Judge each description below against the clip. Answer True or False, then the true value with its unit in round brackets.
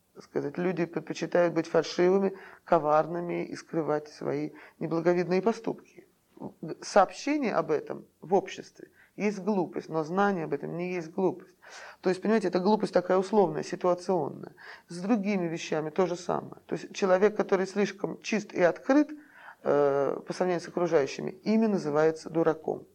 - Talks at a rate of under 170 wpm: True (145 wpm)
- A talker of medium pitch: True (180 Hz)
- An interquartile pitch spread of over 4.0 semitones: False (3.3 semitones)